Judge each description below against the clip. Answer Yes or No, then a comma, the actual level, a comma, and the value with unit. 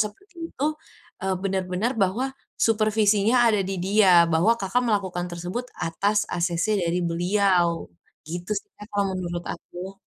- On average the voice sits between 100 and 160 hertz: No, high, 195 Hz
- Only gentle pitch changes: No, average, 3.3 semitones